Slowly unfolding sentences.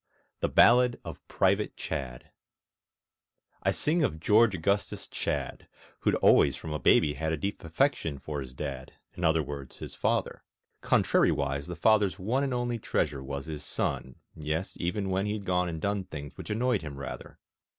No: average, 170 wpm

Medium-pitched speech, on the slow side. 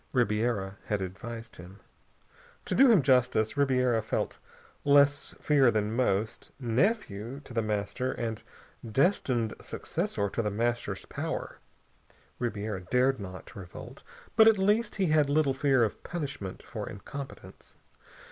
No: low, 120 Hz; slow, 130 wpm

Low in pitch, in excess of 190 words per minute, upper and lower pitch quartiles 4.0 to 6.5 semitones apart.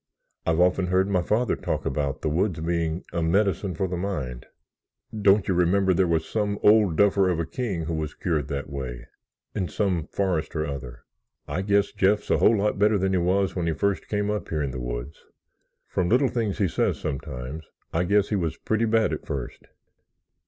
Yes: very low, 90 Hz; average, 200 wpm; average, 4.3 semitones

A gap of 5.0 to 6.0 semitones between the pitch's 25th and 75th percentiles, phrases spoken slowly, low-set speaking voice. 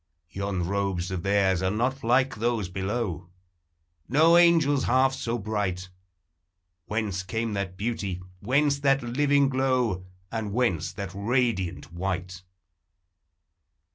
Yes: average, 5.3 semitones; slow, 115 wpm; low, 105 Hz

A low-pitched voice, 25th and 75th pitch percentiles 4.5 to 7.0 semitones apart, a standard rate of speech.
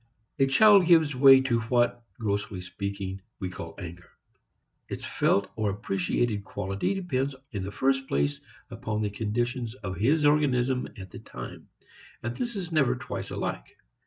Yes: low, 120 Hz; average, 5.3 semitones; average, 155 wpm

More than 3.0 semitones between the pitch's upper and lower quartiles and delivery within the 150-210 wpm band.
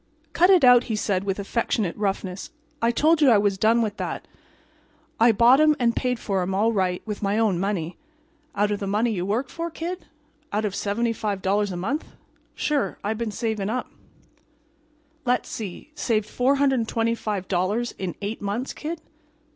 Yes: average, 3.6 semitones; average, 165 wpm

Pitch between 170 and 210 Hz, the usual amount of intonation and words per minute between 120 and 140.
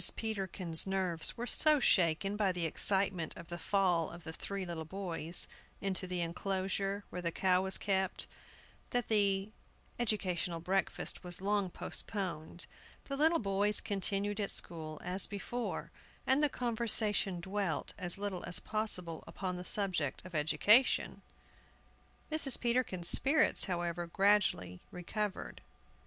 Yes: high, 190 Hz; average, 3.0 semitones; slow, 135 wpm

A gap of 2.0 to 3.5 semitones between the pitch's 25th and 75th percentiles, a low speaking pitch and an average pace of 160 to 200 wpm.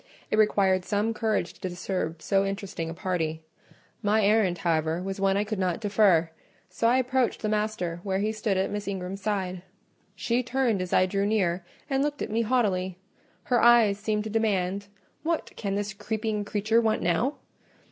No: average, 2.9 semitones; high, 205 Hz; average, 180 wpm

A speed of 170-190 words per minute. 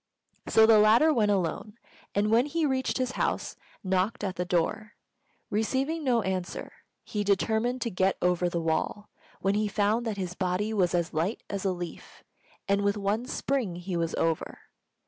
Yes: average, 175 wpm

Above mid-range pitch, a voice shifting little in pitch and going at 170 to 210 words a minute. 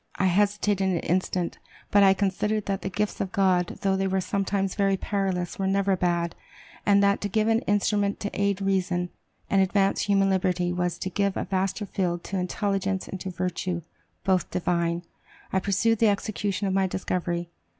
Yes: high, 195 Hz; narrow, 1.7 semitones; average, 180 wpm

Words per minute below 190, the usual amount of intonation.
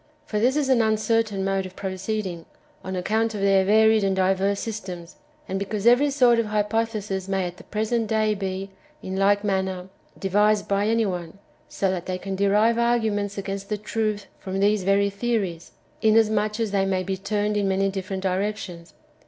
No: average, 180 wpm; narrow, 2.1 semitones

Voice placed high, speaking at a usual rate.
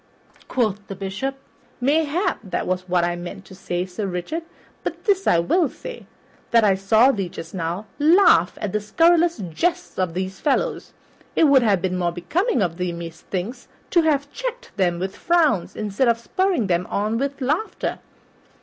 Yes: high, 210 Hz; average, 175 wpm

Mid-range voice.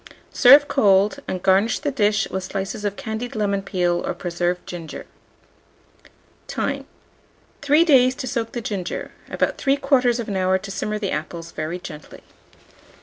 No: high, 205 Hz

